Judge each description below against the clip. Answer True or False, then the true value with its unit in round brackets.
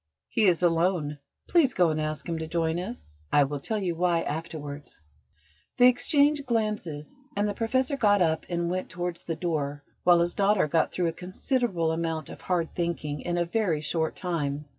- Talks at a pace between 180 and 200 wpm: True (185 wpm)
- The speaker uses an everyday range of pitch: True (4.2 semitones)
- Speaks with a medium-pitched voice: True (170 Hz)